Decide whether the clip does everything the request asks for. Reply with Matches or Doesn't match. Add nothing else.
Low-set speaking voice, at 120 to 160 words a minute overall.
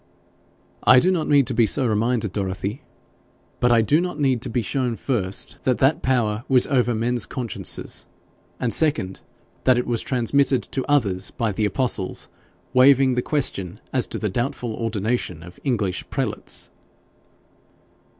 Matches